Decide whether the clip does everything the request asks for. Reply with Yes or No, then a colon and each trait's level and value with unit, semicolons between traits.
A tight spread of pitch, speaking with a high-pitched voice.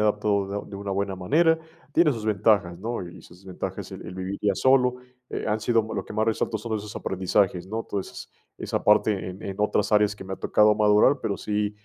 No: narrow, 2.1 semitones; low, 105 Hz